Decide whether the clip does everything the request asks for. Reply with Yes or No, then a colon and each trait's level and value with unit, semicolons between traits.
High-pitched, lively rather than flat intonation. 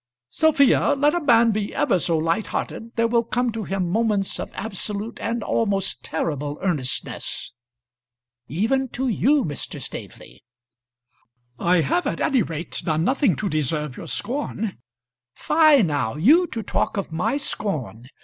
Yes: high, 205 Hz; wide, 6.9 semitones